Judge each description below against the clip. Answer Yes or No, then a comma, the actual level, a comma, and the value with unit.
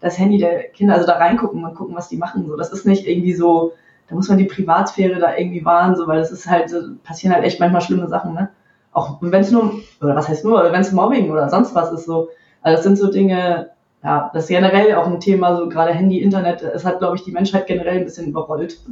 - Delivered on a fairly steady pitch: Yes, narrow, 2.3 semitones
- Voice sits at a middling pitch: Yes, medium, 175 Hz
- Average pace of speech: No, fast, 255 wpm